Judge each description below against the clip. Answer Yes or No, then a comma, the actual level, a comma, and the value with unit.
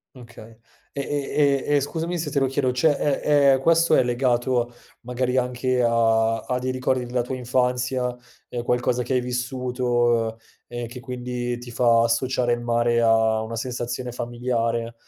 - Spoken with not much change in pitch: Yes, narrow, 1.5 semitones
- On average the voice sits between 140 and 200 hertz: No, low, 125 Hz